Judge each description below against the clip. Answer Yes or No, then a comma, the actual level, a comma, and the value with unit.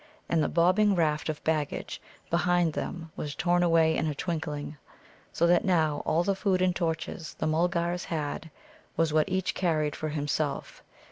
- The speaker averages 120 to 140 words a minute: No, average, 165 wpm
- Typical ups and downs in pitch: No, narrow, 2.3 semitones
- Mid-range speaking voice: Yes, medium, 165 Hz